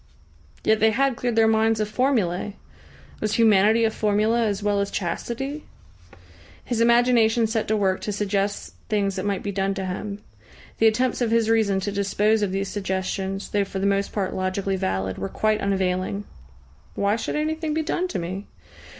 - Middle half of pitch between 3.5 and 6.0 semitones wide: No, narrow, 2.5 semitones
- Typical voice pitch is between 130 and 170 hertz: No, high, 210 Hz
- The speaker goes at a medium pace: Yes, average, 180 wpm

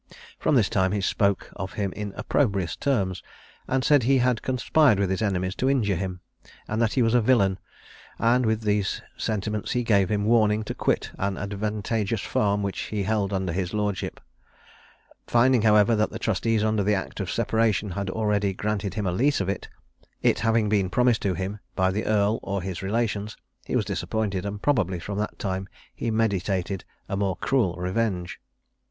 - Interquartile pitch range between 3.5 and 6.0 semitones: No, narrow, 2.6 semitones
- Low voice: Yes, low, 105 Hz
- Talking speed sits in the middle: Yes, average, 185 wpm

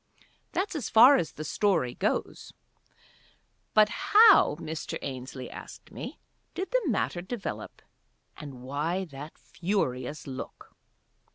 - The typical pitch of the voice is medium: Yes, medium, 170 Hz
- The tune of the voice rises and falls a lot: Yes, wide, 8.9 semitones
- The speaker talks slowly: Yes, slow, 115 wpm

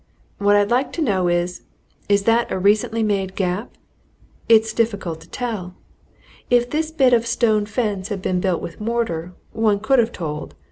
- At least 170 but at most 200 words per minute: Yes, average, 180 wpm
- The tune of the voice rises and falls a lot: No, average, 4.0 semitones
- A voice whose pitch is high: Yes, high, 210 Hz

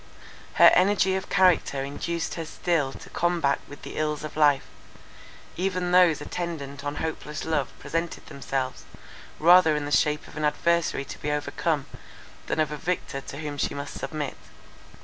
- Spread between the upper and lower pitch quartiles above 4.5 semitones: No, average, 3.1 semitones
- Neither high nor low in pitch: Yes, medium, 155 Hz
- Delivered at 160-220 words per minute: Yes, average, 165 wpm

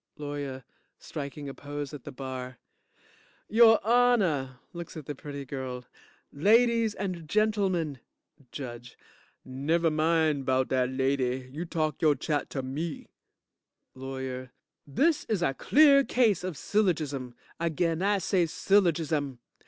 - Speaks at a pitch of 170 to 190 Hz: No, medium, 150 Hz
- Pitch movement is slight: No, wide, 5.6 semitones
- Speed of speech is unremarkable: No, slow, 125 wpm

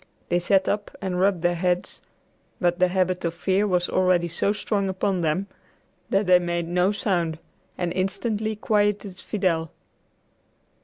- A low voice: No, medium, 185 Hz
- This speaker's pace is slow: No, average, 150 wpm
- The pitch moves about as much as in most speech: No, narrow, 2.2 semitones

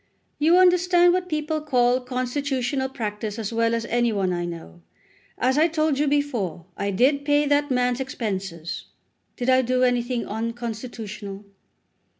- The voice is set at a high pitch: Yes, very high, 250 Hz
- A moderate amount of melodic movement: Yes, average, 4.8 semitones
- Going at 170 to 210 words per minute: No, average, 150 wpm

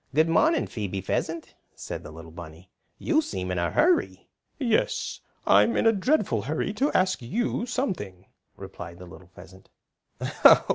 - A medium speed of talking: Yes, average, 150 wpm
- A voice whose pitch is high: No, low, 135 Hz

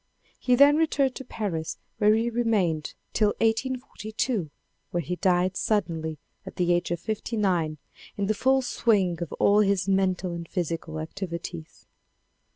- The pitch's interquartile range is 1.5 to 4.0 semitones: No, average, 4.6 semitones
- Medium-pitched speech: No, high, 195 Hz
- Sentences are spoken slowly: No, average, 150 wpm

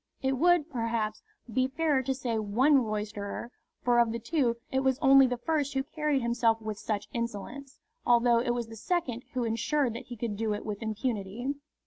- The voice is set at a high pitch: Yes, high, 240 Hz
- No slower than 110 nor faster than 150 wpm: No, average, 190 wpm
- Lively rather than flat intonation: No, average, 3.2 semitones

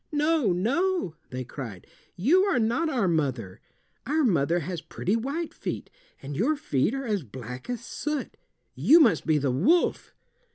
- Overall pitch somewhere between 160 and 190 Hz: No, high, 215 Hz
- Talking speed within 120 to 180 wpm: Yes, average, 160 wpm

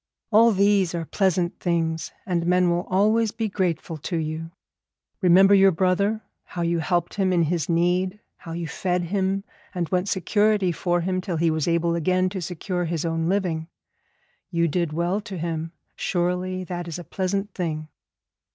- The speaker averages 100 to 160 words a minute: No, average, 170 wpm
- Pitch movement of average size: No, narrow, 2.2 semitones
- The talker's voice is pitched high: No, medium, 180 Hz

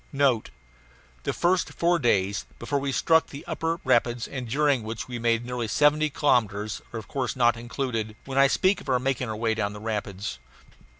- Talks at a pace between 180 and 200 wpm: Yes, average, 190 wpm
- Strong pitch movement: No, average, 4.1 semitones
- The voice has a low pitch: Yes, low, 125 Hz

